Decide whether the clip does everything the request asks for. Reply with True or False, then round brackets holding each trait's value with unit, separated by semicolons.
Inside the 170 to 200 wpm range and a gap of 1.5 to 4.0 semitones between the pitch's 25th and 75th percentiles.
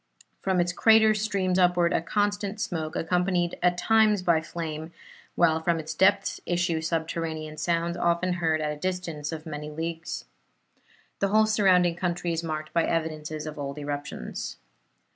False (155 wpm; 2.5 semitones)